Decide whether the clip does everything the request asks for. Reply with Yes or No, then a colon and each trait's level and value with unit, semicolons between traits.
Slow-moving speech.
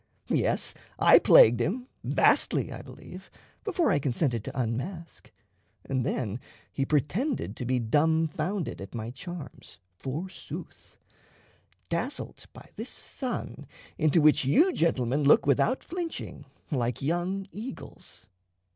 Yes: slow, 120 wpm